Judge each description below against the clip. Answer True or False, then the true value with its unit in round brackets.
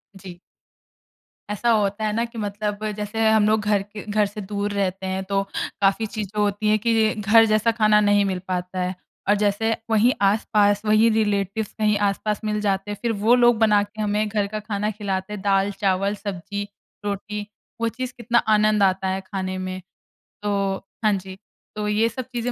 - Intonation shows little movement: True (1.5 semitones)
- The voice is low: False (205 Hz)